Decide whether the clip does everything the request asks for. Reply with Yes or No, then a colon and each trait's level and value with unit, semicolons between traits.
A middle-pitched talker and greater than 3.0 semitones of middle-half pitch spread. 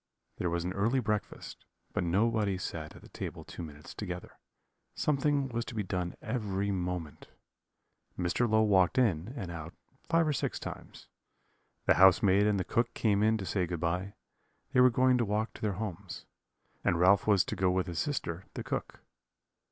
No: low, 100 Hz; average, 4.0 semitones